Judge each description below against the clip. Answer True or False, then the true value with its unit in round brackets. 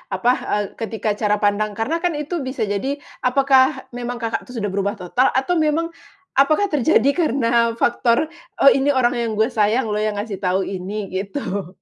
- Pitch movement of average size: True (4.8 semitones)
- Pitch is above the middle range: True (235 Hz)